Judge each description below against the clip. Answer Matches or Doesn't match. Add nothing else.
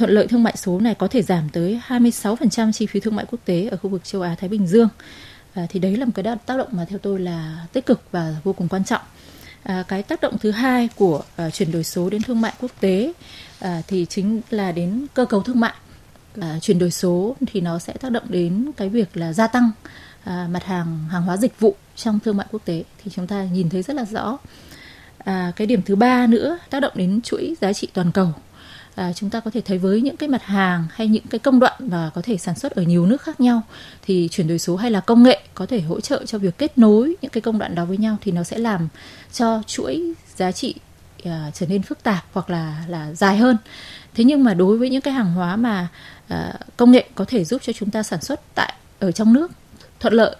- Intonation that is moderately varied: Matches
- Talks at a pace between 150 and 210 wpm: Doesn't match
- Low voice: Doesn't match